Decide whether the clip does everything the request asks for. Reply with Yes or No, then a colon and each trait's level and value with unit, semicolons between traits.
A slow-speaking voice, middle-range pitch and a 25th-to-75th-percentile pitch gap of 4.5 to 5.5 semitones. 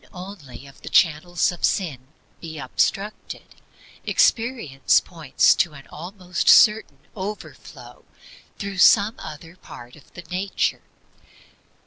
Yes: slow, 120 wpm; medium, 175 Hz; average, 4.8 semitones